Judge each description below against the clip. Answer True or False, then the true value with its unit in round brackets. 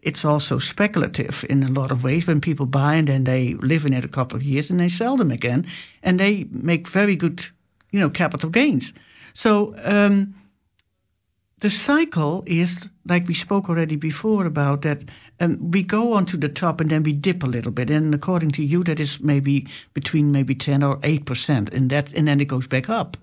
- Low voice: False (150 Hz)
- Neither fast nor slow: False (210 wpm)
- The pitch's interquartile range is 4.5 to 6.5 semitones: True (4.8 semitones)